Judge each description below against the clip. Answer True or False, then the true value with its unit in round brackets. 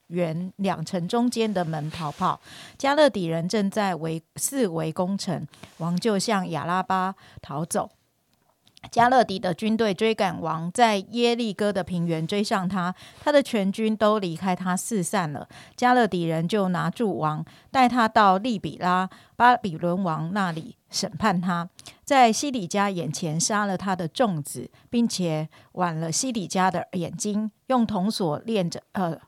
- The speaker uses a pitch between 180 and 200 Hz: True (185 Hz)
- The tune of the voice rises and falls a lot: False (4.6 semitones)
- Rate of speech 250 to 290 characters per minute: False (225 characters per minute)